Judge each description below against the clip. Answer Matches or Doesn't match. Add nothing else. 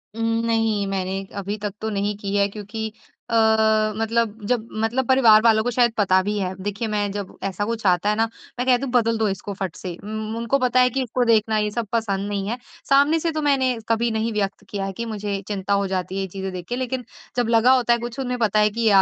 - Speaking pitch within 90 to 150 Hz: Doesn't match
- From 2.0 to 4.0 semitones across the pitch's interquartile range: Matches